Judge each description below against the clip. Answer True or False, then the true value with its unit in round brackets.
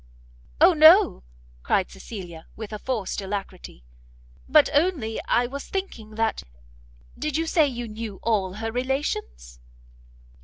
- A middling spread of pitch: False (6.6 semitones)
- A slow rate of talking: True (125 wpm)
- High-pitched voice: True (225 Hz)